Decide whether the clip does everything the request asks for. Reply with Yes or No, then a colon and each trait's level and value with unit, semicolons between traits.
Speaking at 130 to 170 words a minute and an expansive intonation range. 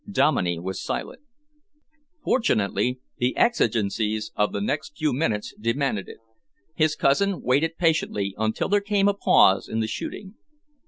Yes: average, 140 wpm; wide, 7.6 semitones